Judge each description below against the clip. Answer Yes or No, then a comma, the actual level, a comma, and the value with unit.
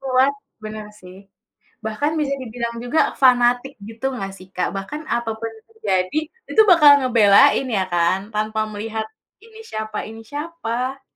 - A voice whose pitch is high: Yes, high, 230 Hz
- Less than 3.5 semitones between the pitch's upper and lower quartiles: No, average, 4.2 semitones